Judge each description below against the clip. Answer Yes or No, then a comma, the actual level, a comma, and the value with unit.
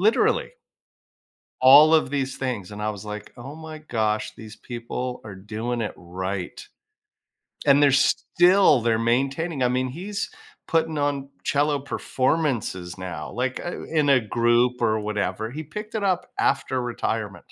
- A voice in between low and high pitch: No, low, 125 Hz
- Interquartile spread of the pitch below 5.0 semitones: No, average, 5.3 semitones